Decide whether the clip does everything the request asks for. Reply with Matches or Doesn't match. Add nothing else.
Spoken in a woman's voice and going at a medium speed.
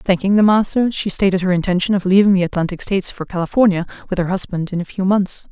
Doesn't match